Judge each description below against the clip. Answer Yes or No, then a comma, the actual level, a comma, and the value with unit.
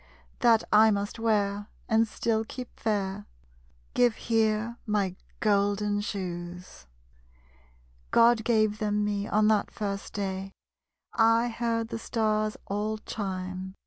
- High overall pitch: Yes, high, 210 Hz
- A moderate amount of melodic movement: No, narrow, 1.9 semitones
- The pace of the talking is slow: Yes, slow, 115 wpm